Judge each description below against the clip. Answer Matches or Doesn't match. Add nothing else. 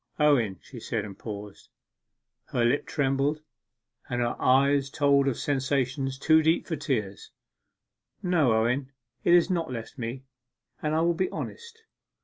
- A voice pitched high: Doesn't match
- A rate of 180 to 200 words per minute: Doesn't match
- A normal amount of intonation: Matches